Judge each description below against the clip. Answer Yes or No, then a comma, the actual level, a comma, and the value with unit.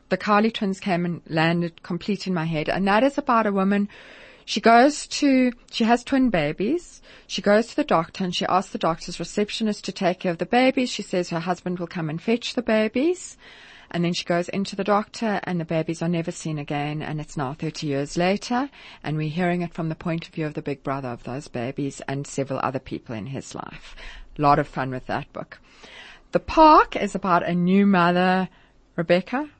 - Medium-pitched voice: Yes, medium, 180 Hz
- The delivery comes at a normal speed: No, fast, 220 wpm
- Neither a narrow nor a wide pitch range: Yes, average, 4.7 semitones